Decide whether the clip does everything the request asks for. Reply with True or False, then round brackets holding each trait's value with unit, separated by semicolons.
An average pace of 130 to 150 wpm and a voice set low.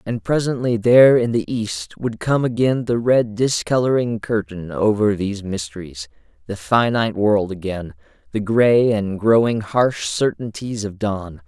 True (145 wpm; 110 Hz)